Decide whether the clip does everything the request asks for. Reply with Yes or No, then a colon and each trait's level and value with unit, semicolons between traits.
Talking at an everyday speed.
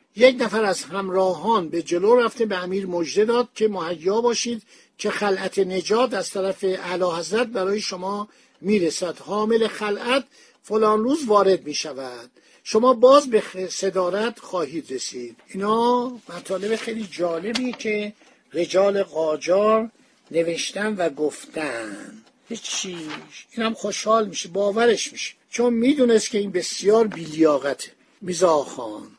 Yes: average, 130 wpm